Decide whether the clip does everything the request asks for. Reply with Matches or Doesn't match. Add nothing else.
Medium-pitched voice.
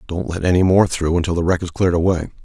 Doesn't match